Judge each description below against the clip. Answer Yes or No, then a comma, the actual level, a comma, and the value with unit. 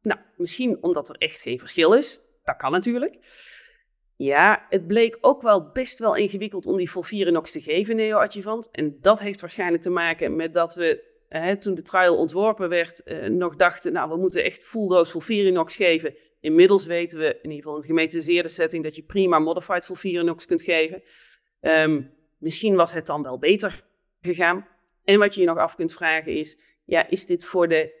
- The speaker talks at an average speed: Yes, average, 190 wpm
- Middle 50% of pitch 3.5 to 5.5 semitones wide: Yes, average, 4.0 semitones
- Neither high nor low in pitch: Yes, medium, 180 Hz